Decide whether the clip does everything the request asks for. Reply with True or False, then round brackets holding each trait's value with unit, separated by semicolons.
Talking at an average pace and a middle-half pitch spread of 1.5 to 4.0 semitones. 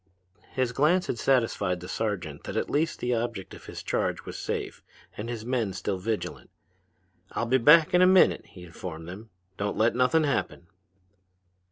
False (175 wpm; 5.2 semitones)